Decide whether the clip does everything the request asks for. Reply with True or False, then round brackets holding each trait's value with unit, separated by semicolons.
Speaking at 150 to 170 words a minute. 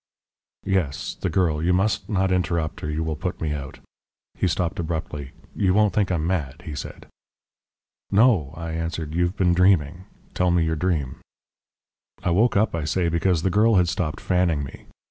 False (180 wpm)